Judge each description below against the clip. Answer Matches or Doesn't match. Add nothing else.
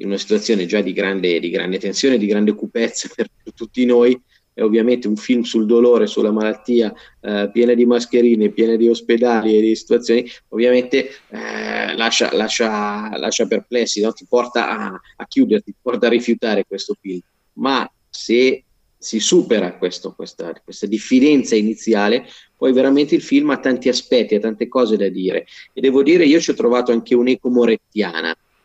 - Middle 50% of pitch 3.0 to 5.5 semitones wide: Doesn't match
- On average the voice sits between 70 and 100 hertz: Doesn't match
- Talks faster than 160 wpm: Matches